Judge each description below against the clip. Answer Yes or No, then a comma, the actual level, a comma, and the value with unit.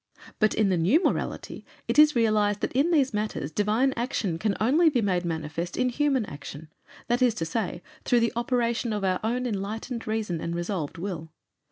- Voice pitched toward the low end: No, high, 215 Hz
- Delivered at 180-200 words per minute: Yes, average, 190 wpm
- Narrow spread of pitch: No, wide, 5.5 semitones